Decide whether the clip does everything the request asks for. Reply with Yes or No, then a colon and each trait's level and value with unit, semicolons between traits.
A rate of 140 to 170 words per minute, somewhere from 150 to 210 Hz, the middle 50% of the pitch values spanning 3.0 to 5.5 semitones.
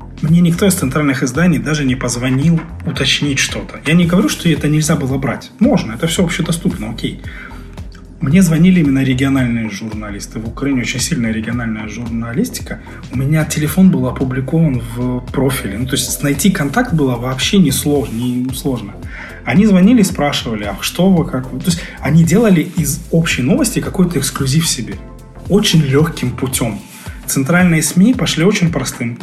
No: fast, 160 wpm; medium, 140 Hz; average, 5.0 semitones